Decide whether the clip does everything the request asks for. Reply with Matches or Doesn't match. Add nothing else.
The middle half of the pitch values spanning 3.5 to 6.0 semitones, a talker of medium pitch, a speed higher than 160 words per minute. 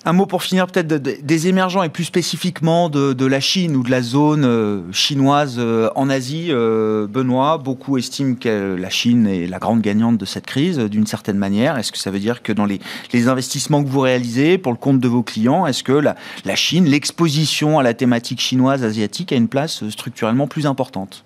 Doesn't match